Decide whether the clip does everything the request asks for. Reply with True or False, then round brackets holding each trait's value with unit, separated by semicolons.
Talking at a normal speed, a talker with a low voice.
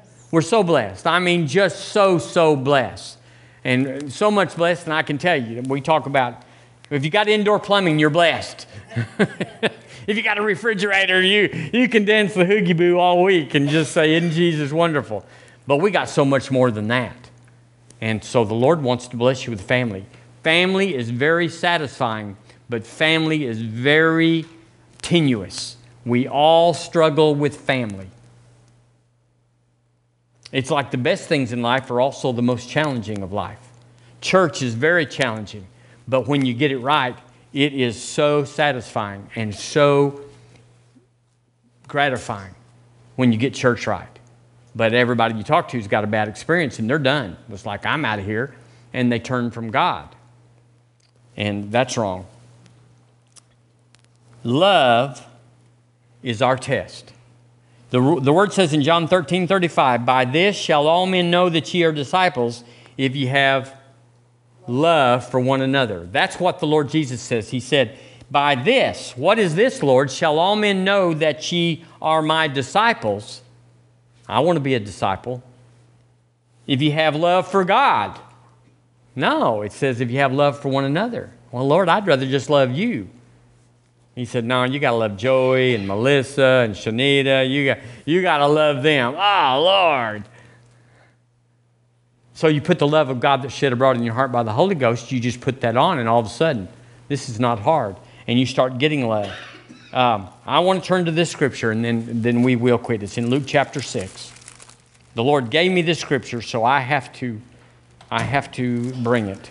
True (170 wpm; 125 Hz)